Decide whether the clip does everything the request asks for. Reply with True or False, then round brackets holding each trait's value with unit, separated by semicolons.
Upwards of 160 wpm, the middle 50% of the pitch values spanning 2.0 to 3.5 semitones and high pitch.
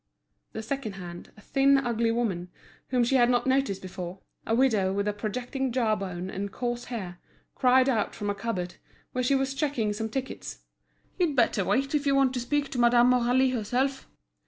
False (190 wpm; 4.4 semitones; 240 Hz)